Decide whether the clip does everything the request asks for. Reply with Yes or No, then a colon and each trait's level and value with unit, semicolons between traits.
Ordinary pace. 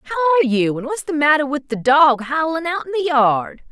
No: fast, 240 wpm